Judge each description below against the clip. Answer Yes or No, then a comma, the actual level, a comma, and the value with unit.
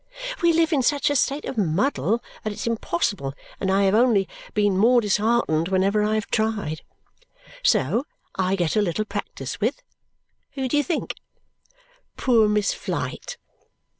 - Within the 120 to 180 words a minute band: Yes, average, 155 wpm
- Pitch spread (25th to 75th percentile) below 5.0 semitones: Yes, average, 4.5 semitones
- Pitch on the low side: No, high, 215 Hz